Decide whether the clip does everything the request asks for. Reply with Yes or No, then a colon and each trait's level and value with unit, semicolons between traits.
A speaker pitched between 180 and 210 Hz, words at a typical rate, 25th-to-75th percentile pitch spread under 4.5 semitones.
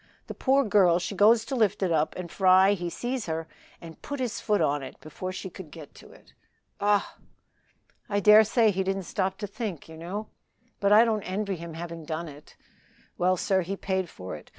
No: high, 190 Hz; fast, 210 wpm; average, 3.7 semitones